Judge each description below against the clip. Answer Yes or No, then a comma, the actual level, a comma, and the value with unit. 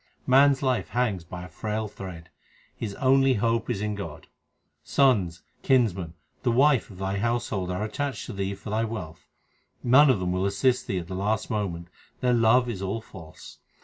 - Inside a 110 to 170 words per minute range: No, average, 185 wpm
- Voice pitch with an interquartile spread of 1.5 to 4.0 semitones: No, average, 4.7 semitones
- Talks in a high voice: No, low, 105 Hz